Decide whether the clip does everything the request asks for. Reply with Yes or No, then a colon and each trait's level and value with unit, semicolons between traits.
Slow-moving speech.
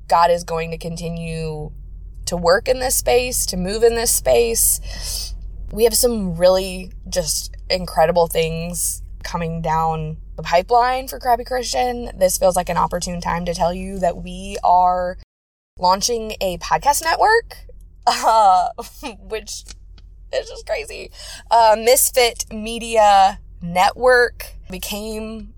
Yes: slow, 130 wpm